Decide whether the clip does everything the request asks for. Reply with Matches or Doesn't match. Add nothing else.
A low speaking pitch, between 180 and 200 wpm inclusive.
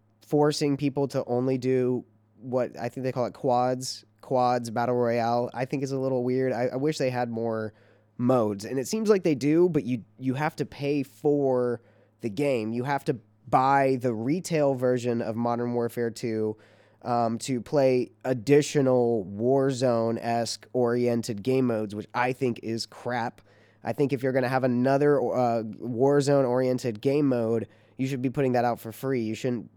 Matches